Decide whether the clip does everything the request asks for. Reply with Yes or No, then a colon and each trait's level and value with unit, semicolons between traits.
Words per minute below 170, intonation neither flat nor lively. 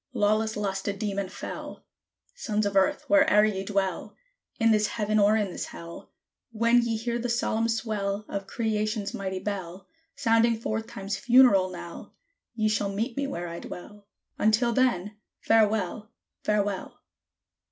No: average, 150 wpm; narrow, 2.3 semitones